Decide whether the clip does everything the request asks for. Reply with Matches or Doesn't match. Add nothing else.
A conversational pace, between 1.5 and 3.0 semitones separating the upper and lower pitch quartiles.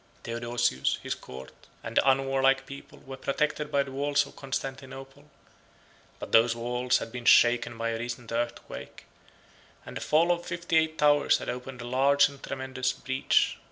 Matches